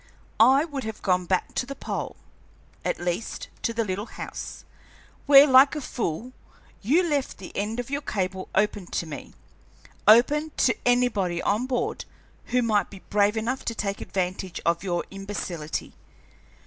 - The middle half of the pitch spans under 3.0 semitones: No, average, 5.3 semitones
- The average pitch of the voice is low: No, high, 220 Hz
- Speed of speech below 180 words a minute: Yes, average, 160 wpm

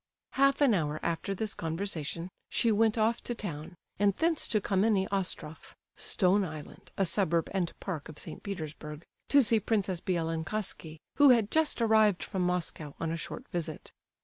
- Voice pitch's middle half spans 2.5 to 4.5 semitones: No, average, 4.9 semitones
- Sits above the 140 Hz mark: Yes, high, 190 Hz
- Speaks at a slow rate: No, average, 170 wpm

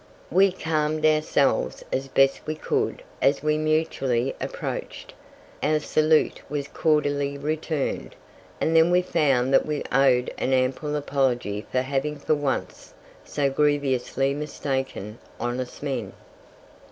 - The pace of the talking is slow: Yes, slow, 125 wpm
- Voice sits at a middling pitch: Yes, medium, 145 Hz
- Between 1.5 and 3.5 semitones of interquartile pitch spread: Yes, narrow, 2.5 semitones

